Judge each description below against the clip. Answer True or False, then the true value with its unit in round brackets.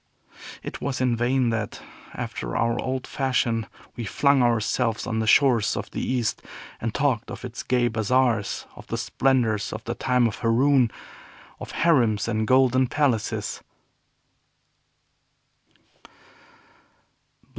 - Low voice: True (120 Hz)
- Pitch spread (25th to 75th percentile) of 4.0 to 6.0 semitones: False (2.5 semitones)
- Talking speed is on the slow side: True (125 wpm)